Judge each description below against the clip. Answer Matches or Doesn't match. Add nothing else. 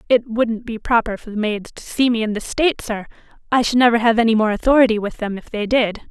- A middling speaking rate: Doesn't match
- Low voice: Doesn't match